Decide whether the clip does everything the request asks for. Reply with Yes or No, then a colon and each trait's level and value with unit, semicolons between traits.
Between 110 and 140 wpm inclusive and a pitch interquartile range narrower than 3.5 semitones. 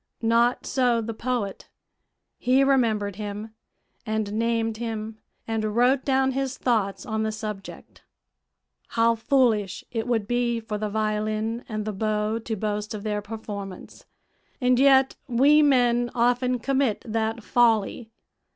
Yes: slow, 135 wpm; narrow, 2.4 semitones